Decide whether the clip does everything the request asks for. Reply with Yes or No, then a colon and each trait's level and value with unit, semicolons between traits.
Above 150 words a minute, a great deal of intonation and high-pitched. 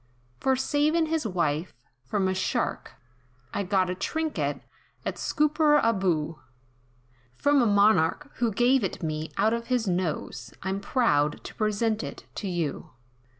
No: average, 140 wpm; wide, 6.5 semitones; high, 205 Hz